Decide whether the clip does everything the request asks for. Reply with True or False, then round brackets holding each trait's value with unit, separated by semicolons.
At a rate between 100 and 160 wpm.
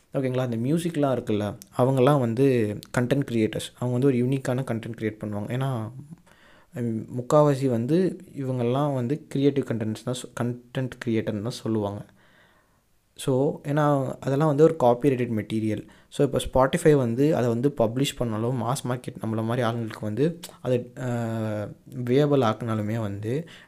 True (130 wpm)